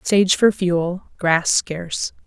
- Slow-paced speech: Yes, slow, 130 wpm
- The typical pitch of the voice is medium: Yes, medium, 180 Hz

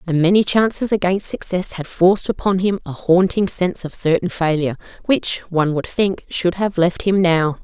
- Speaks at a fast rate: No, average, 190 wpm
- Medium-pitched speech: Yes, medium, 180 Hz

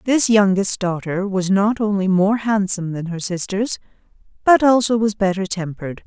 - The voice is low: No, high, 200 Hz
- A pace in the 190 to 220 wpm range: No, average, 160 wpm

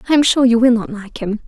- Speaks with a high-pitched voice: Yes, high, 235 Hz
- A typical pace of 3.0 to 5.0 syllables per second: No, 6.5 syllables/s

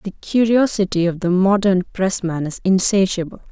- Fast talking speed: No, slow, 135 wpm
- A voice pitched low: No, high, 190 Hz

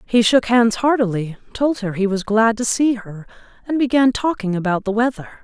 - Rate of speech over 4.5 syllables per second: Yes, 5.0 syllables/s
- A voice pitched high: Yes, high, 225 Hz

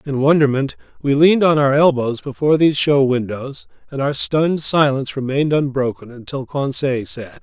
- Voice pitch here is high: No, medium, 140 Hz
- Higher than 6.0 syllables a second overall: No, 5.4 syllables/s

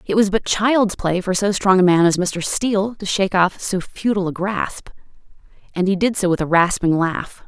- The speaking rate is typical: No, fast, 225 wpm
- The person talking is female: Yes, female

